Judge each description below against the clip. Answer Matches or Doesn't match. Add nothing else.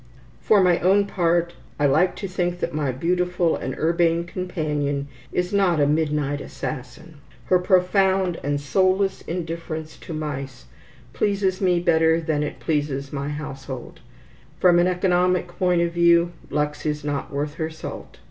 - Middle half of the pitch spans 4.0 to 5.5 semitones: Doesn't match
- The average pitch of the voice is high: Doesn't match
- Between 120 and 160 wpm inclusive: Matches